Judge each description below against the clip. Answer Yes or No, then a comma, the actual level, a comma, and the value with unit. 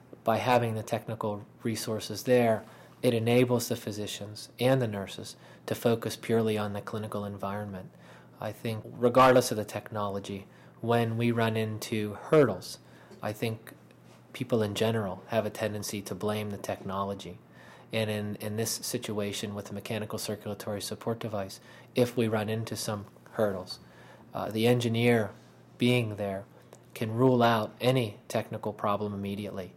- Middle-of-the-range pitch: No, low, 110 Hz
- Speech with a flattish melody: Yes, narrow, 2.2 semitones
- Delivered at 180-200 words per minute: No, average, 145 wpm